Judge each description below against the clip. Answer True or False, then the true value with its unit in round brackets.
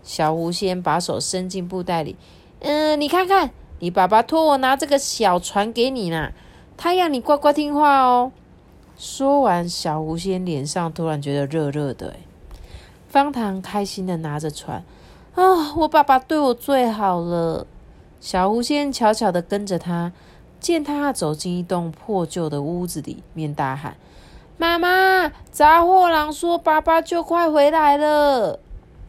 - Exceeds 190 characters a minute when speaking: True (215 characters per minute)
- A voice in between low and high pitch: False (215 Hz)